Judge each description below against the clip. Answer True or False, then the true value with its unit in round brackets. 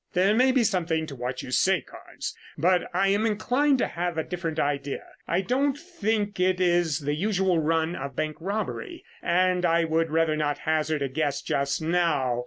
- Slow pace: False (190 wpm)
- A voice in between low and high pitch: True (170 Hz)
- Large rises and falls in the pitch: False (4.2 semitones)